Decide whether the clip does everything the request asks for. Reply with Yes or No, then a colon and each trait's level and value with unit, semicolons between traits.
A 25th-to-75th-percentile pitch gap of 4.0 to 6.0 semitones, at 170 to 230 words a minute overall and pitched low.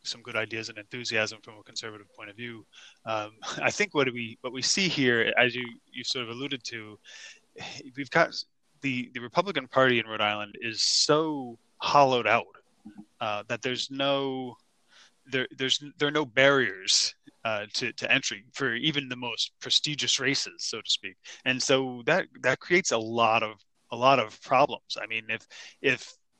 No: average, 3.6 semitones; average, 180 wpm; low, 125 Hz